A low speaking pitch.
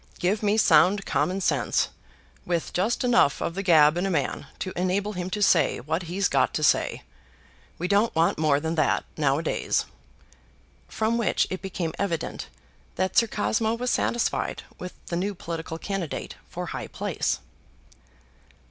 No: medium, 180 Hz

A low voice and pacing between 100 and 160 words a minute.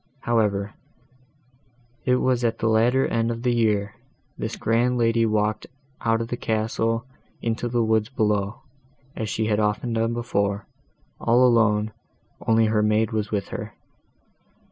Yes: low, 115 Hz; average, 145 wpm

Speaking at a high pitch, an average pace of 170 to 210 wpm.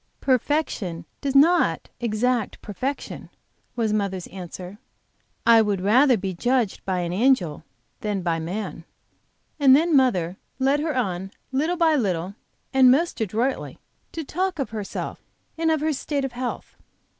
No: high, 240 Hz; average, 145 wpm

